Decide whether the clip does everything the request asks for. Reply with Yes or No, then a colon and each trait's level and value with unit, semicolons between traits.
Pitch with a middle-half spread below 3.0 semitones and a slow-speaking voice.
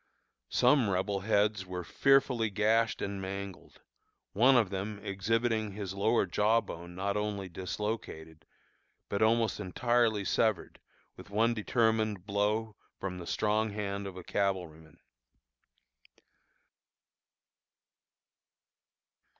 Yes: narrow, 2.6 semitones; slow, 105 wpm